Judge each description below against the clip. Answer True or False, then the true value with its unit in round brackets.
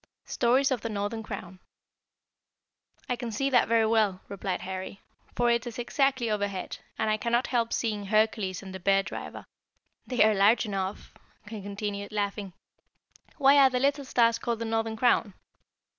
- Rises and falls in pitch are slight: False (3.1 semitones)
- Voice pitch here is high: True (220 Hz)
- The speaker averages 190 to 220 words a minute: False (165 wpm)